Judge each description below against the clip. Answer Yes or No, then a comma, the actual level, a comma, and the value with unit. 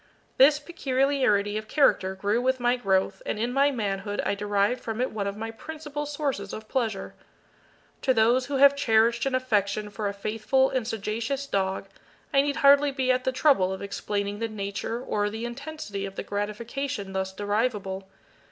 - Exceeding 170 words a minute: Yes, average, 180 wpm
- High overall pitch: Yes, high, 225 Hz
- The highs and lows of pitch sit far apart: No, average, 4.7 semitones